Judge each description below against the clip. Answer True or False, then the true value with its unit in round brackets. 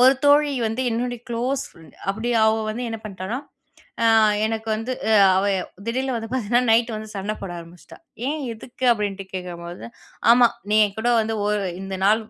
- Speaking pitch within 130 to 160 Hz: False (225 Hz)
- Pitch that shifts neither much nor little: True (3.3 semitones)